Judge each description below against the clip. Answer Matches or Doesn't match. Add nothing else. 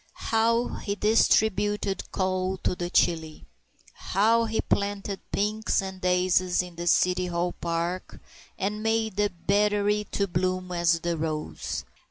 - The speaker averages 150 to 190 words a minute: Doesn't match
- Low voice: Doesn't match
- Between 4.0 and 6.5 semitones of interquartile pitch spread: Doesn't match